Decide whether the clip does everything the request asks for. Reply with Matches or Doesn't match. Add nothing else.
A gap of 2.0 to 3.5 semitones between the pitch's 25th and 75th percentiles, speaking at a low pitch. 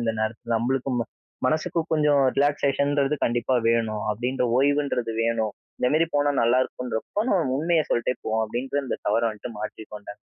Doesn't match